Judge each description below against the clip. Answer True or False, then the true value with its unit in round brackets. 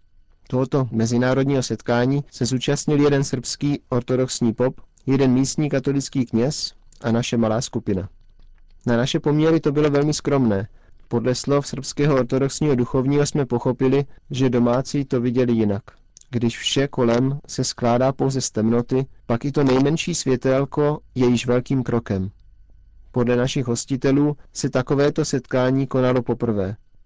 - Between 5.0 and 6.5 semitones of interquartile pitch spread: False (2.9 semitones)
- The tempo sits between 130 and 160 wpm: True (135 wpm)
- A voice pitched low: True (130 Hz)